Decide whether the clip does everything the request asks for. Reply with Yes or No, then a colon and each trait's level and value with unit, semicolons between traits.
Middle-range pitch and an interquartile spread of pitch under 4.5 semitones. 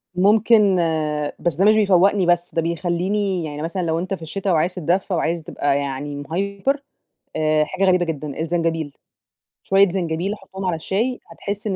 Yes: medium, 175 Hz; average, 3.4 semitones